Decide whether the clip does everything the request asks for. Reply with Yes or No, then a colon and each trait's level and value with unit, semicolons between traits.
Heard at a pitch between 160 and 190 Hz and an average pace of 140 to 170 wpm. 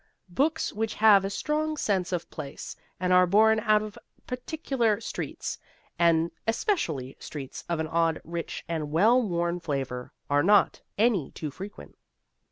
Yes: medium, 185 Hz; average, 150 wpm